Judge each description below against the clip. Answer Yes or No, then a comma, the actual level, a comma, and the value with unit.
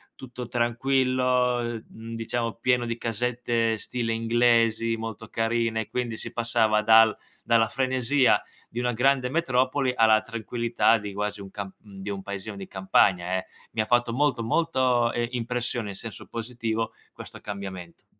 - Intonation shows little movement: Yes, narrow, 1.9 semitones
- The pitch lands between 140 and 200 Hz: No, low, 115 Hz